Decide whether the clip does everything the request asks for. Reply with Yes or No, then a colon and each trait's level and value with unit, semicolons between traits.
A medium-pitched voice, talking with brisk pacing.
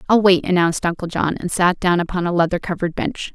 Yes: medium, 175 Hz; fast, 235 wpm